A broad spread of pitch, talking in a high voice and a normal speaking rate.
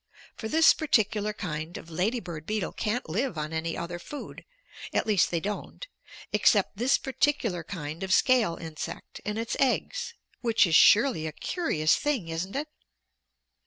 Yes: wide, 7.0 semitones; high, 205 Hz; average, 160 wpm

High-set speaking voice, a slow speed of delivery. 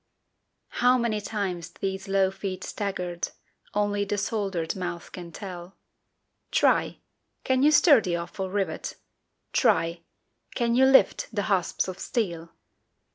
Yes: high, 195 Hz; slow, 130 wpm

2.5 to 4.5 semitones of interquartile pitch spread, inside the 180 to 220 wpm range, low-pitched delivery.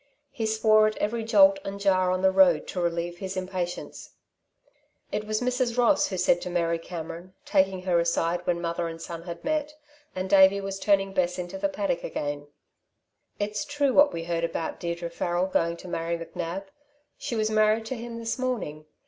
No: average, 4.0 semitones; average, 190 wpm; high, 190 Hz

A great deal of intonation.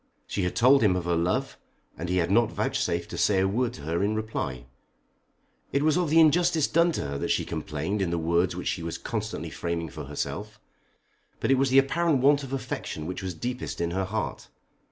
Yes: wide, 8.0 semitones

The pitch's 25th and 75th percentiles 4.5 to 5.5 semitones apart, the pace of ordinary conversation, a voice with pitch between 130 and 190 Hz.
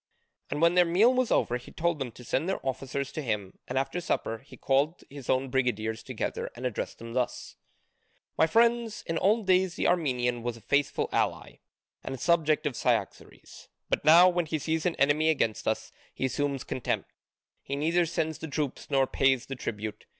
Yes: average, 4.9 semitones; average, 190 wpm; medium, 140 Hz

